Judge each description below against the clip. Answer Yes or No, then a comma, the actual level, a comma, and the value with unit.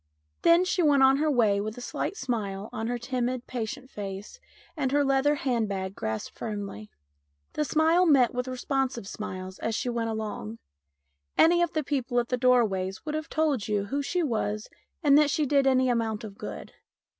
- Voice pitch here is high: Yes, very high, 250 Hz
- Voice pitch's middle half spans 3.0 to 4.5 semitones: No, average, 5.1 semitones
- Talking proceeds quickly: No, average, 190 wpm